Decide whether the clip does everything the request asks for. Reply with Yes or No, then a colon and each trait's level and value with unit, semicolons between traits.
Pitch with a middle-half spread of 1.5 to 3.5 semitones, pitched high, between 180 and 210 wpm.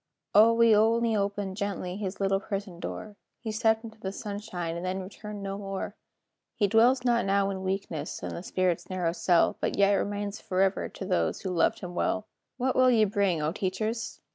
Yes: narrow, 2.5 semitones; high, 200 Hz; average, 190 wpm